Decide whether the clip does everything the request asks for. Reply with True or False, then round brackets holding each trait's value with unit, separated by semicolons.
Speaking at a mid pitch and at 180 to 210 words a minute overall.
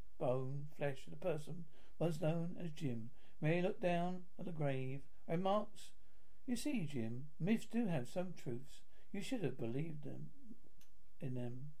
False (160 Hz; 165 wpm)